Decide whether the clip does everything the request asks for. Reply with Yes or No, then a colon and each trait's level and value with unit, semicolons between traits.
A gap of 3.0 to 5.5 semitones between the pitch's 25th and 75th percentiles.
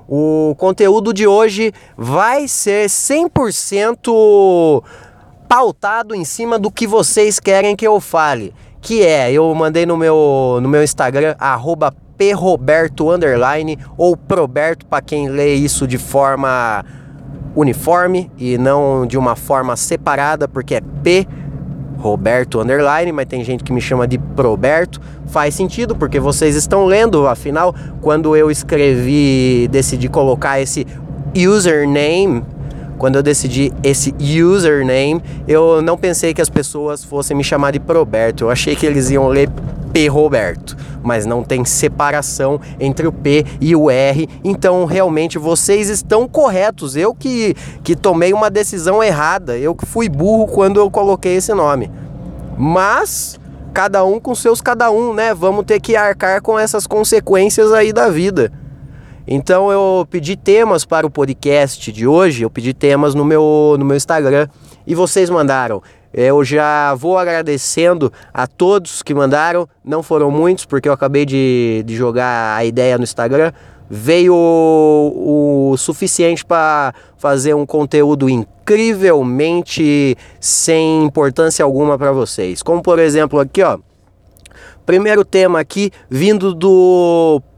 Yes: average, 5.1 semitones